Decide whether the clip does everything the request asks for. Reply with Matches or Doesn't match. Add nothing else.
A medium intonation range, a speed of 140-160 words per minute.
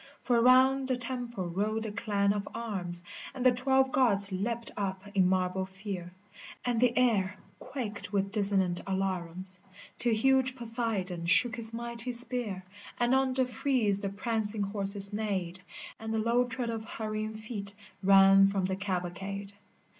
Matches